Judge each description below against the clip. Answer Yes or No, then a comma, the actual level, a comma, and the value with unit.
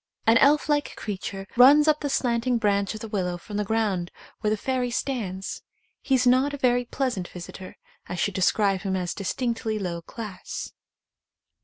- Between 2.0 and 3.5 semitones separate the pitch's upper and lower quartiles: No, average, 4.8 semitones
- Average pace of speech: Yes, average, 180 wpm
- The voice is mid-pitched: No, high, 220 Hz